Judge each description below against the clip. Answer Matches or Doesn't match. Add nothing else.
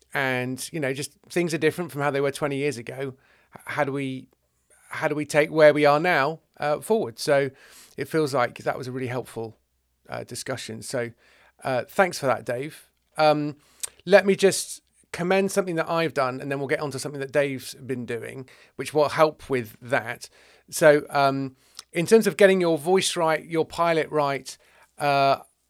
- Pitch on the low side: Doesn't match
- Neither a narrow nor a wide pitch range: Matches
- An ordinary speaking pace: Matches